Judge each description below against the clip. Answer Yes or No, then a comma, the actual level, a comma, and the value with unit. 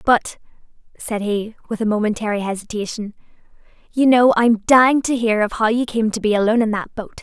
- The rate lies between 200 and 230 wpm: No, average, 190 wpm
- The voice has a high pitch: Yes, high, 220 Hz